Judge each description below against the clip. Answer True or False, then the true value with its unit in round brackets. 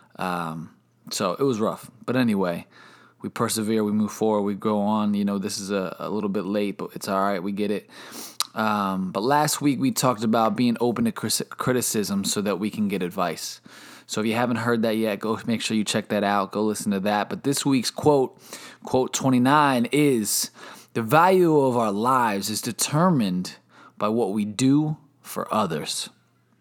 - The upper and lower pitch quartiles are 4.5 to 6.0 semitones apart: True (5.2 semitones)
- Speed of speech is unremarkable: True (195 wpm)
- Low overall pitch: True (110 Hz)